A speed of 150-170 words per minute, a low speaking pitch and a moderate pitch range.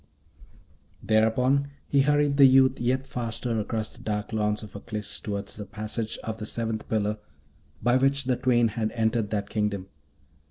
Yes: average, 160 wpm; low, 110 Hz; average, 3.2 semitones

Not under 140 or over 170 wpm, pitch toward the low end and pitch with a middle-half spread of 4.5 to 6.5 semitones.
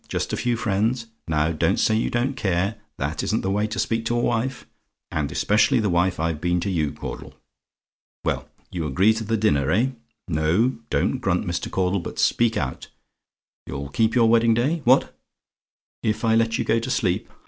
No: average, 190 wpm; low, 110 Hz; average, 5.1 semitones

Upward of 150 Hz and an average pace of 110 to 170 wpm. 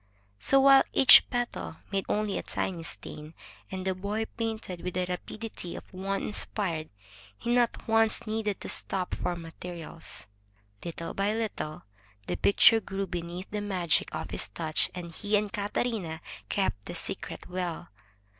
Yes: high, 190 Hz; average, 155 wpm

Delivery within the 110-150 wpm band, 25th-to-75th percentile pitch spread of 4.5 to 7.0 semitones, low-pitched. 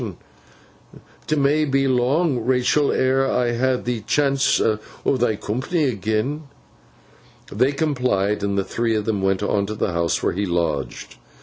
Yes: average, 145 wpm; average, 5.0 semitones; low, 120 Hz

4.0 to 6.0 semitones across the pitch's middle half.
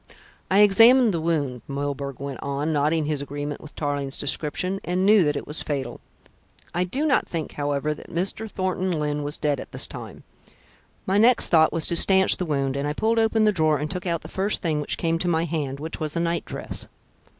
Yes: average, 4.3 semitones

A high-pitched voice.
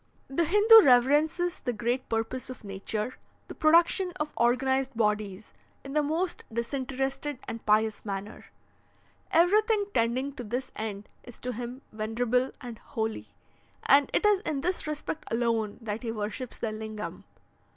Yes: very high, 250 Hz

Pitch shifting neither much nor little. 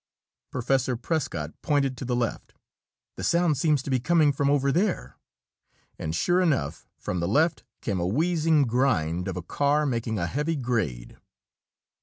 No: wide, 7.4 semitones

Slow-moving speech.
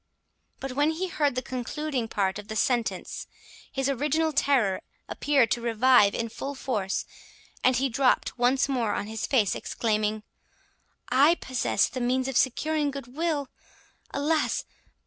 No: average, 145 wpm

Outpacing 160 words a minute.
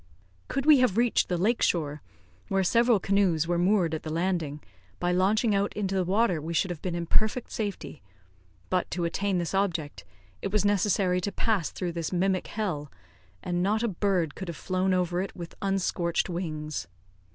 Yes: average, 185 wpm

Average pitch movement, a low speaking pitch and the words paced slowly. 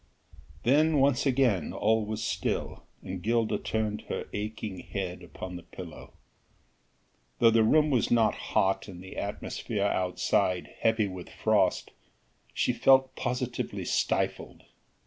Yes: average, 4.5 semitones; low, 110 Hz; slow, 125 wpm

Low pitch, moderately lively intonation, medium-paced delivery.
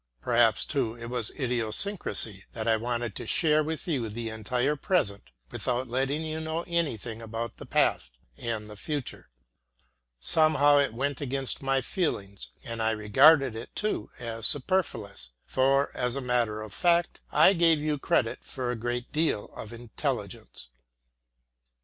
Yes: low, 125 Hz; average, 4.9 semitones; average, 150 wpm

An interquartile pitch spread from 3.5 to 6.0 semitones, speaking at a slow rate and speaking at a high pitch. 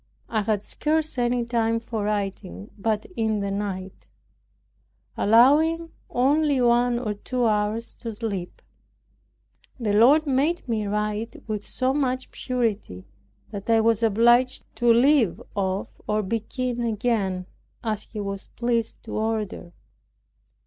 No: average, 2.9 semitones; slow, 130 wpm; high, 225 Hz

